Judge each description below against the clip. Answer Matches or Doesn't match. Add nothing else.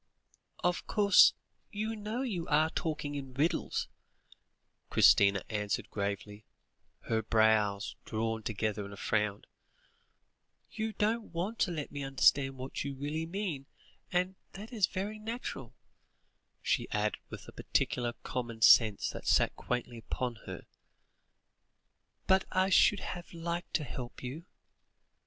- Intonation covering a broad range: Matches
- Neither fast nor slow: Doesn't match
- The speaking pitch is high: Doesn't match